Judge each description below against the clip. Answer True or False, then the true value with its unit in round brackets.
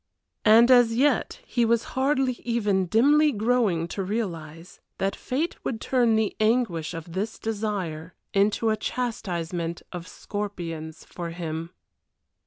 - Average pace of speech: False (130 wpm)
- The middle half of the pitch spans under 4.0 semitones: False (5.6 semitones)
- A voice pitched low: False (210 Hz)